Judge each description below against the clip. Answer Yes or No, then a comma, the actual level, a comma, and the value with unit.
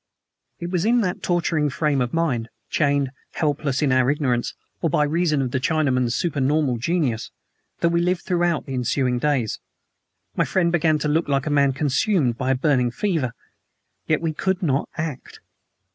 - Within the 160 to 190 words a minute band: Yes, average, 175 wpm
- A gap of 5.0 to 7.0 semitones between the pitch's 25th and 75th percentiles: No, average, 4.4 semitones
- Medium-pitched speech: Yes, medium, 150 Hz